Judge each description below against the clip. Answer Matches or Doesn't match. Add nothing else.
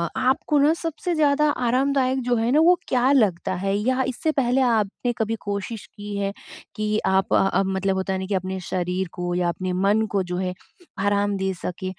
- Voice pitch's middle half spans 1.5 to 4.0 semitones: Doesn't match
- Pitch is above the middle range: Matches